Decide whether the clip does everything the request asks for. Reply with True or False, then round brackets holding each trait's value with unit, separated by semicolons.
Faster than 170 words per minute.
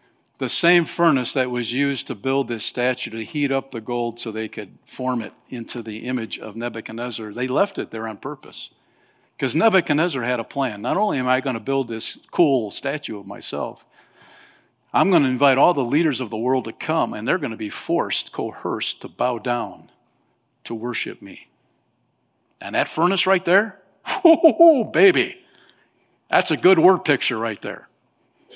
True (185 wpm)